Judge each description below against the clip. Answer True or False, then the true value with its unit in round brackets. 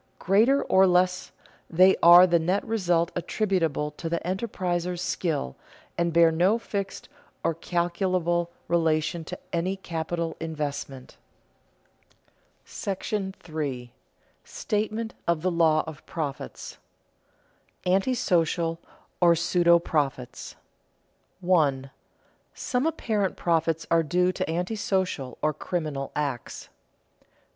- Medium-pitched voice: True (170 Hz)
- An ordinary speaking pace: False (105 wpm)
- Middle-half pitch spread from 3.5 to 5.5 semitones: False (2.6 semitones)